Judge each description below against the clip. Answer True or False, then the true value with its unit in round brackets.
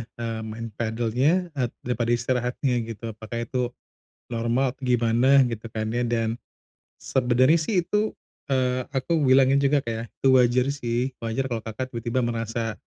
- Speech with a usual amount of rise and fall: False (2.3 semitones)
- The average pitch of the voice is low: True (120 Hz)